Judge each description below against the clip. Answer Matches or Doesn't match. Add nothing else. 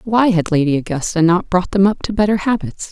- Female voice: Matches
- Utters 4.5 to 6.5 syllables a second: Matches